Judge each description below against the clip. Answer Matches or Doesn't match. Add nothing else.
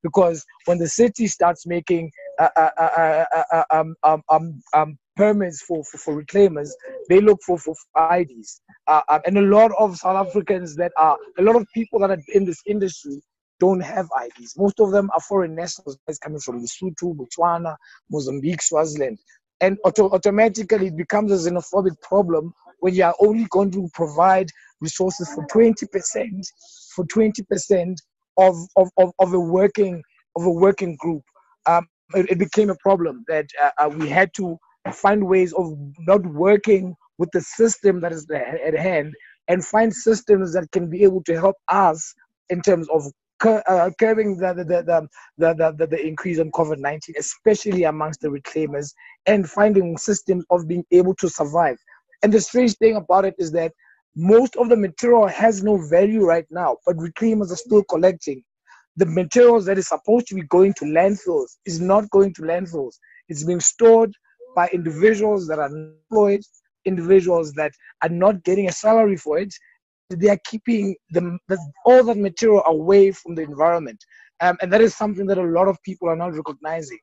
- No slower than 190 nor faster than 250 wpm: Doesn't match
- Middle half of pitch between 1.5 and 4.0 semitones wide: Matches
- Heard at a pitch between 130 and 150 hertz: Doesn't match